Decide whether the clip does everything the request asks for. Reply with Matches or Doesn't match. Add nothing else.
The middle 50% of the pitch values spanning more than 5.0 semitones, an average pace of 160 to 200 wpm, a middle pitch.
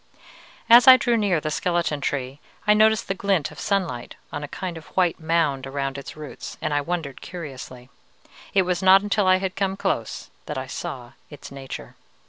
Matches